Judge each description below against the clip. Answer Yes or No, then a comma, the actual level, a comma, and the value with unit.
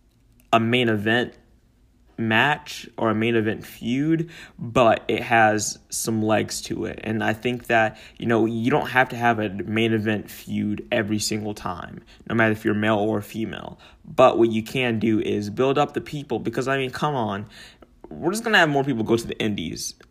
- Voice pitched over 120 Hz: No, low, 115 Hz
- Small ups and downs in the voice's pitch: Yes, narrow, 2.0 semitones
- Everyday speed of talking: Yes, average, 195 wpm